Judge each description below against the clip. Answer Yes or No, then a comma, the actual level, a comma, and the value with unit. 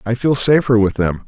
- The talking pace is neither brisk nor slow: No, fast, 235 wpm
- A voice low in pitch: Yes, low, 115 Hz